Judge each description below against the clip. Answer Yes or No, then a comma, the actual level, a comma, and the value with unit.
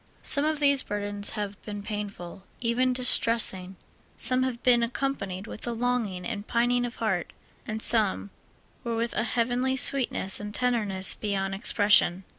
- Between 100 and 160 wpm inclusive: Yes, average, 150 wpm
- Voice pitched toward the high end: Yes, high, 230 Hz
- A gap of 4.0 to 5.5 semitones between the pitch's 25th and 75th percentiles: No, average, 3.4 semitones